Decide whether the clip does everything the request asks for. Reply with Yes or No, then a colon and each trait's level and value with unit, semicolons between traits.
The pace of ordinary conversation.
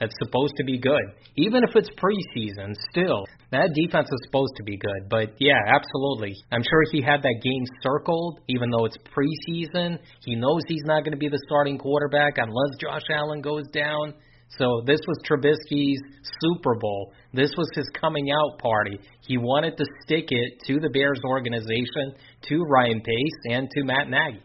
Yes: average, 180 wpm